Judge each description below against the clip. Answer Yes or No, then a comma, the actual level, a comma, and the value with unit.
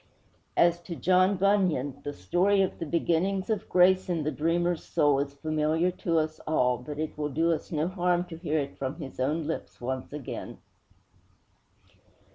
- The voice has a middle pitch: Yes, medium, 160 Hz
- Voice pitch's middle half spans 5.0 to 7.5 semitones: No, average, 3.3 semitones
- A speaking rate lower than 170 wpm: No, average, 175 wpm